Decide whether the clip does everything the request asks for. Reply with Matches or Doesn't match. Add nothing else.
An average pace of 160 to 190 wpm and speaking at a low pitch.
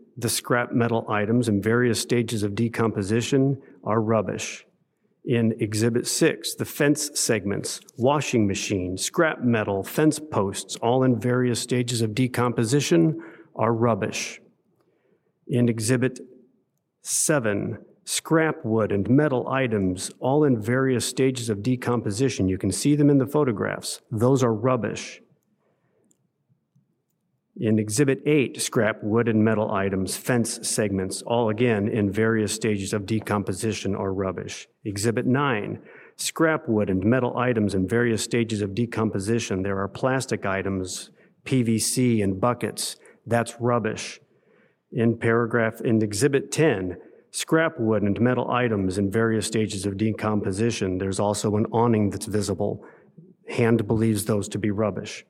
Doesn't match